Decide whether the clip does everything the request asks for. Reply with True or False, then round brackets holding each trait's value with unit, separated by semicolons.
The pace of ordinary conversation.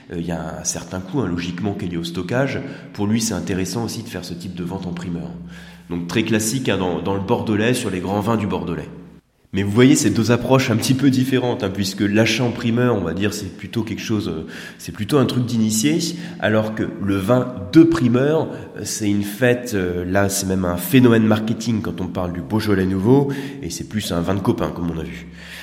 False (235 wpm)